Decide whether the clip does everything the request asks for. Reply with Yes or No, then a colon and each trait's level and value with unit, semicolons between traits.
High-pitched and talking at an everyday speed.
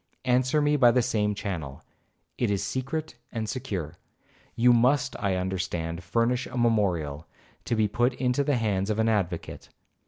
No: low, 110 Hz; average, 160 wpm